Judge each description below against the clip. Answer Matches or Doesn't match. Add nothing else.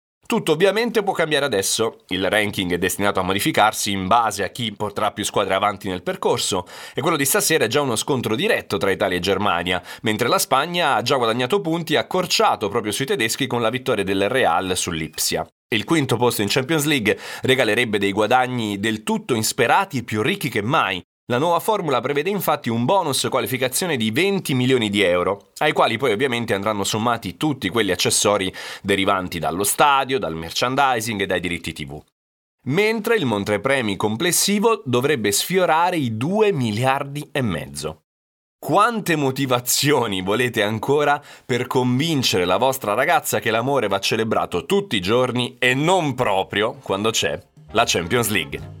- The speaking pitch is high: Doesn't match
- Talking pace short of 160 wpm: Doesn't match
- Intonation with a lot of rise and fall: Matches